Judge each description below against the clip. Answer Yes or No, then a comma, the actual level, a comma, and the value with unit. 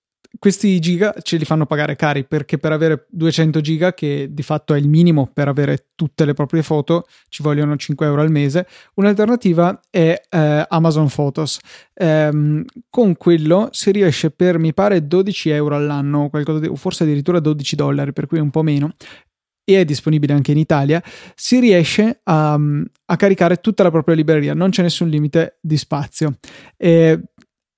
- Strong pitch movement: No, average, 3.0 semitones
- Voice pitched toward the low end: No, medium, 160 Hz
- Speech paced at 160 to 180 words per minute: Yes, fast, 170 wpm